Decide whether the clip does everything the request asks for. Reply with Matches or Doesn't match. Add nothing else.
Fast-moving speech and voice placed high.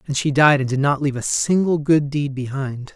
Doesn't match